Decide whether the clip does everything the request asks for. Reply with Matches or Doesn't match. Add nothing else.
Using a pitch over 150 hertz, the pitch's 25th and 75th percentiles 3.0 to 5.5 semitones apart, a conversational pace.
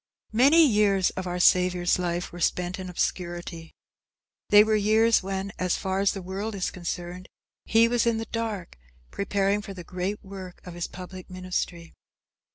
Doesn't match